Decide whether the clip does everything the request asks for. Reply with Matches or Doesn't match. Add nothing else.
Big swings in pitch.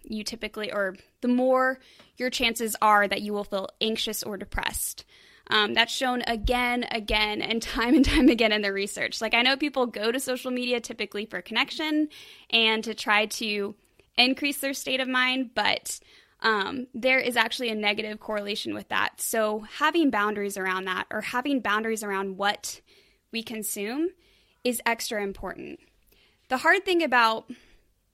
Doesn't match